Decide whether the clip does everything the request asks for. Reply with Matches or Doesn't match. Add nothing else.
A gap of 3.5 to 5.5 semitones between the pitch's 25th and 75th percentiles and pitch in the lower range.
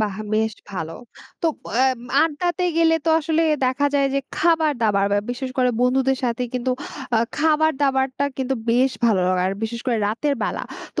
Doesn't match